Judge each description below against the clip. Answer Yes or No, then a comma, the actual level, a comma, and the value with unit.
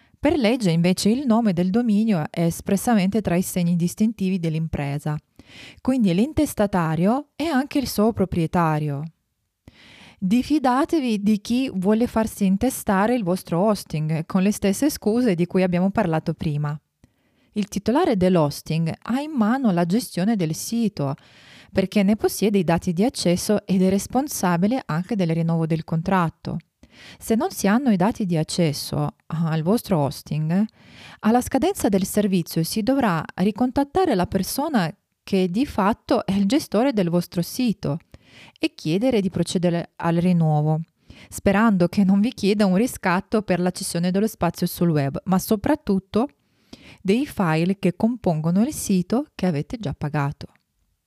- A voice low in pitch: No, high, 195 Hz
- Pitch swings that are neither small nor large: Yes, average, 4.6 semitones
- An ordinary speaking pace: Yes, average, 145 wpm